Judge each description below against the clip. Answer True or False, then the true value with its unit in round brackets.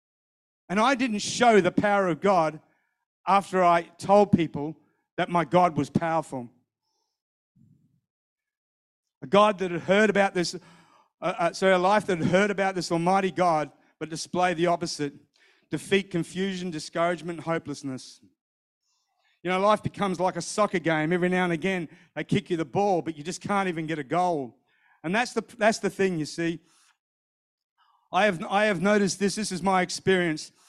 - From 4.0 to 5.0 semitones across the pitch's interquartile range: False (3.3 semitones)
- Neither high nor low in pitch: True (180 Hz)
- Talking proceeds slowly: False (170 wpm)